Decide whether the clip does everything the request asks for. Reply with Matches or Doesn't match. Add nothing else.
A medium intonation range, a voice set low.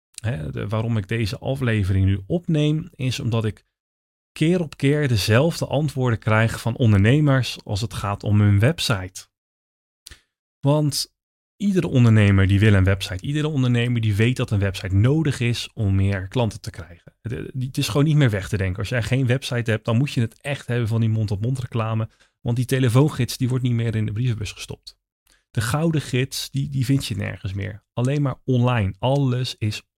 Matches